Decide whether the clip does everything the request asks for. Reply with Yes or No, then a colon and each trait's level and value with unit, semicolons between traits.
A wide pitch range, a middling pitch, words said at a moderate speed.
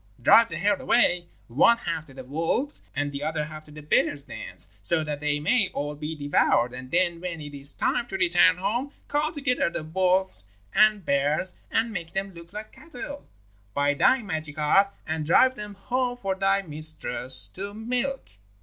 Yes: wide, 5.9 semitones; medium, 175 Hz; average, 185 wpm